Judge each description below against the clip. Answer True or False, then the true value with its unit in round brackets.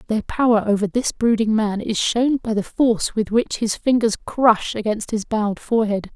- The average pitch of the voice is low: False (220 Hz)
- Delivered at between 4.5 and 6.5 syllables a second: True (5.0 syllables/s)